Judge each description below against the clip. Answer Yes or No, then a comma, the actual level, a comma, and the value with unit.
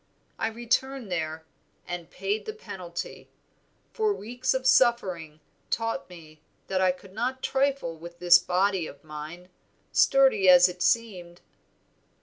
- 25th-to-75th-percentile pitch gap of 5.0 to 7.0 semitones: Yes, wide, 5.6 semitones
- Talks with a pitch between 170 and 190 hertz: Yes, medium, 185 Hz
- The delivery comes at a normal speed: No, slow, 130 wpm